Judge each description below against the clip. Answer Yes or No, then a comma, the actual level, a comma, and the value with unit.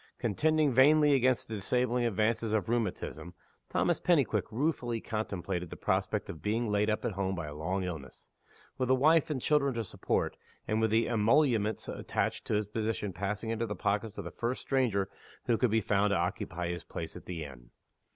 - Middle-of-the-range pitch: No, low, 110 Hz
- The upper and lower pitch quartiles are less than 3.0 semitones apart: No, average, 4.1 semitones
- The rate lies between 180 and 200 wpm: Yes, average, 190 wpm